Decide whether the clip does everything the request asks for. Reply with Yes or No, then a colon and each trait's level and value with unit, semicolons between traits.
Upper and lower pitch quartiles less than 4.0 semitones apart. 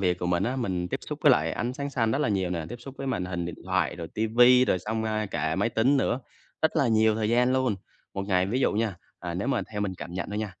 No: average, 5.2 semitones